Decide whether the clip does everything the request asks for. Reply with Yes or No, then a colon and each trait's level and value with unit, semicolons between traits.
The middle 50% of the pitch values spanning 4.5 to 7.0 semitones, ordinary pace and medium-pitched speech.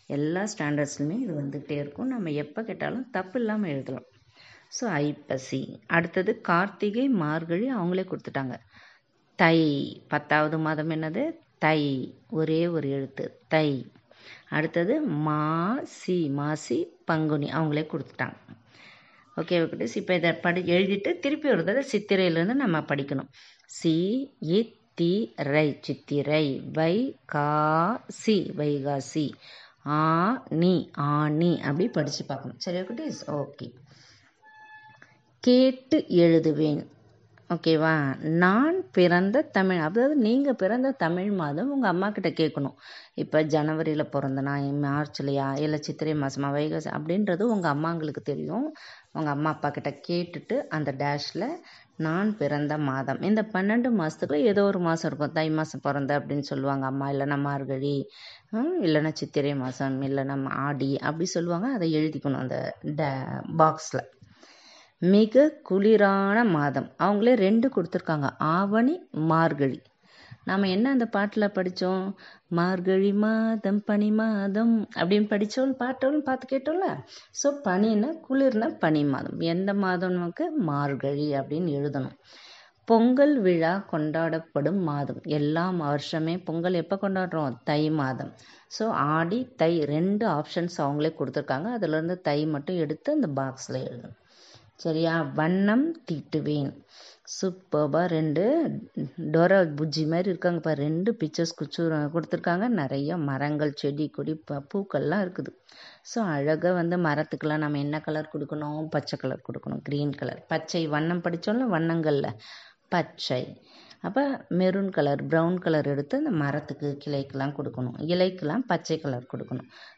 Yes: average, 5.2 semitones; average, 120 wpm; medium, 160 Hz